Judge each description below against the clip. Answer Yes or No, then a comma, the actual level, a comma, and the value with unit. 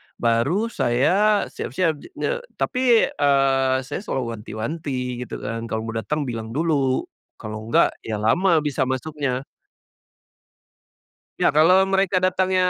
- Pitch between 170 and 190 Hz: No, low, 135 Hz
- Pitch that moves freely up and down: Yes, wide, 7.5 semitones